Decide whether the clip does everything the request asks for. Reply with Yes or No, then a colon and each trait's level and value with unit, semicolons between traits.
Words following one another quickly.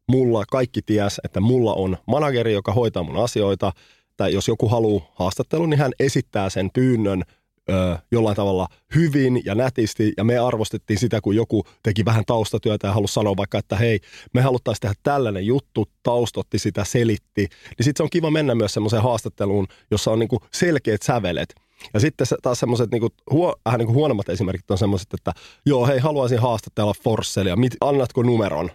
Yes: fast, 175 wpm